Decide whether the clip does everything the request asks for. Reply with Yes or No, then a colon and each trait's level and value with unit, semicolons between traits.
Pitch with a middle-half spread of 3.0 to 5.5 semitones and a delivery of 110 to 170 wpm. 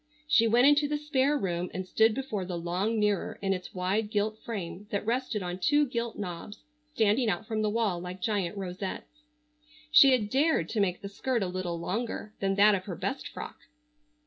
No: average, 4.1 semitones; average, 200 wpm